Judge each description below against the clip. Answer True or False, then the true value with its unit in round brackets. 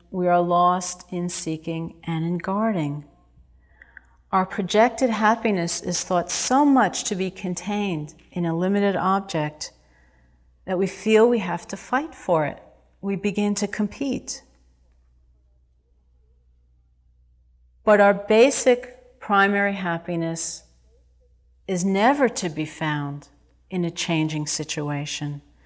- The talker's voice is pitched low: False (175 Hz)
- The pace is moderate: False (115 wpm)